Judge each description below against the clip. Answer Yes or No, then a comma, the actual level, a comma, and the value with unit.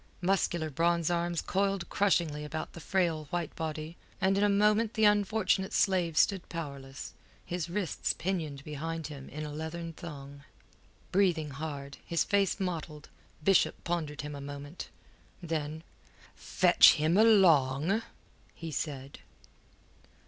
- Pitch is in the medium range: Yes, medium, 165 Hz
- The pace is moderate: No, slow, 130 wpm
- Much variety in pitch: No, average, 4.1 semitones